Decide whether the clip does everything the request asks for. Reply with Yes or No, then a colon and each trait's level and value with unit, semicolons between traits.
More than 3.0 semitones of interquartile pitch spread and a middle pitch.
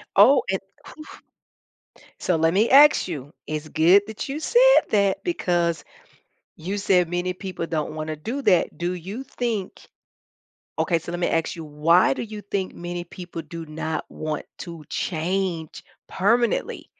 Yes: average, 3.8 semitones; medium, 180 Hz